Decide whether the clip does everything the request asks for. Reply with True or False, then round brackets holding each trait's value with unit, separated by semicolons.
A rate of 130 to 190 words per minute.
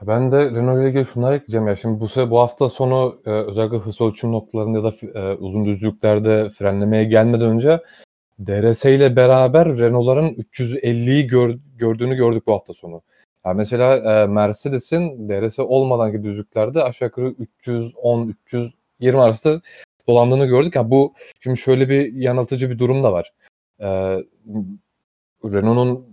True (140 wpm)